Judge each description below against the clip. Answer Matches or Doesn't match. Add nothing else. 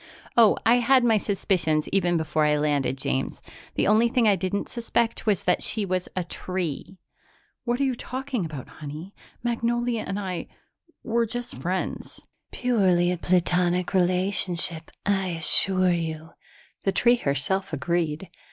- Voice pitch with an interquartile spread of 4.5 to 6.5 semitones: Matches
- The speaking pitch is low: Doesn't match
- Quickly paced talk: Doesn't match